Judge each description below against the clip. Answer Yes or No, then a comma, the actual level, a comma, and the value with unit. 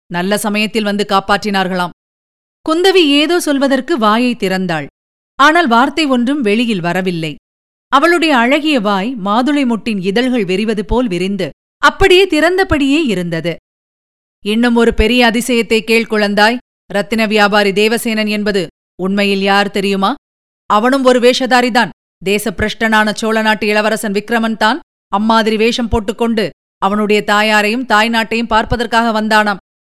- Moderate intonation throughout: Yes, average, 3.2 semitones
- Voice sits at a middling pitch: No, high, 220 Hz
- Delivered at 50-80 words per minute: No, average, 110 wpm